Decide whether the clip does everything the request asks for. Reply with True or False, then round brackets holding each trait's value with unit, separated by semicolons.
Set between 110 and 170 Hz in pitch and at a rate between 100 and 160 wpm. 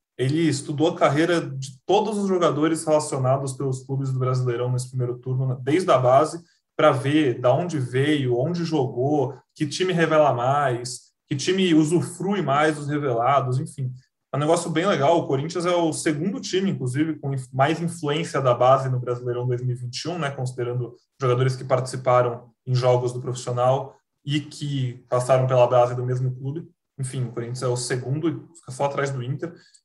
False (135 Hz; 175 wpm)